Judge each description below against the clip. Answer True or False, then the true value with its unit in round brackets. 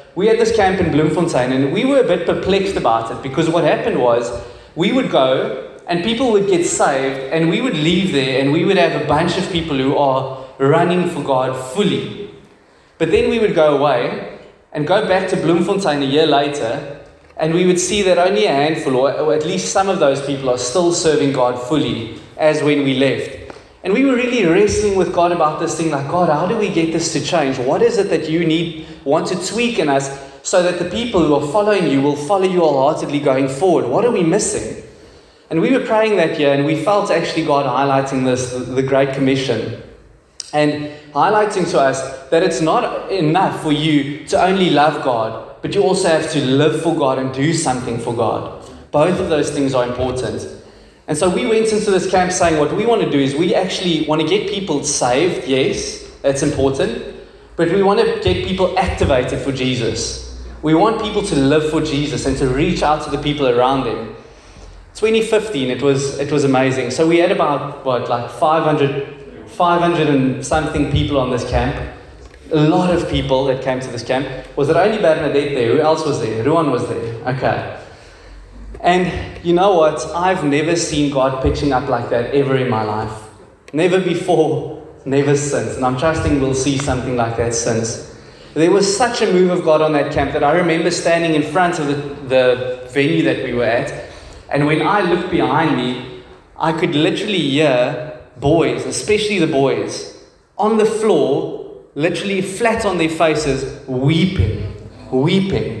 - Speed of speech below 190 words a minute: False (200 wpm)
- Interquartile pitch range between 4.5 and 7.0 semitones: True (4.8 semitones)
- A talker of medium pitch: True (155 Hz)